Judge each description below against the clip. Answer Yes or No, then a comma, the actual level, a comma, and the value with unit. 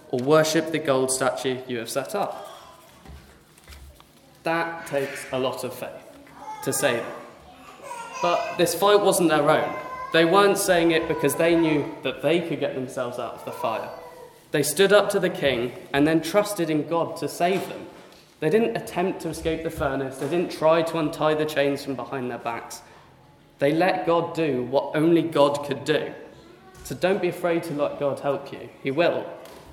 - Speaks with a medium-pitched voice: Yes, medium, 155 Hz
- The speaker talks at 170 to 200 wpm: Yes, average, 185 wpm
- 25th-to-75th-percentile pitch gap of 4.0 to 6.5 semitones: No, average, 3.6 semitones